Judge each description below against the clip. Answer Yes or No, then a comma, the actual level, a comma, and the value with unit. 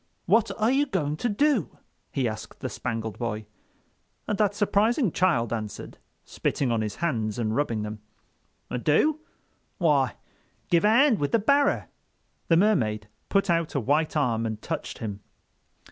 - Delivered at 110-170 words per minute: Yes, average, 155 wpm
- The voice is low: No, medium, 150 Hz